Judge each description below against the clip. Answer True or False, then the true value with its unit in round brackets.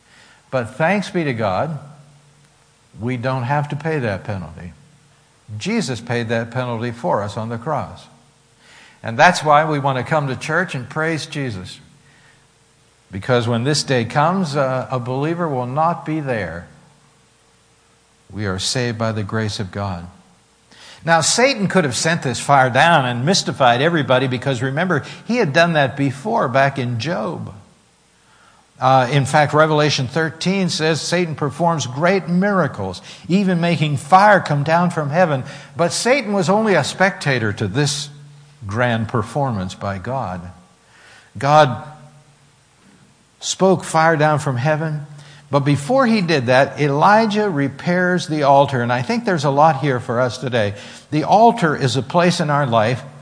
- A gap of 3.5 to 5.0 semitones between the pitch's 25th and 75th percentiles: True (4.4 semitones)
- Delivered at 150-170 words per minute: True (155 wpm)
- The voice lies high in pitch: False (145 Hz)